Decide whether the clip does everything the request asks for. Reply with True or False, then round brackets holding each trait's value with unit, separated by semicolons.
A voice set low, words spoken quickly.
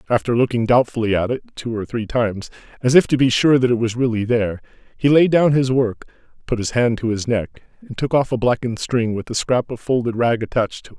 True (120 Hz; 245 wpm)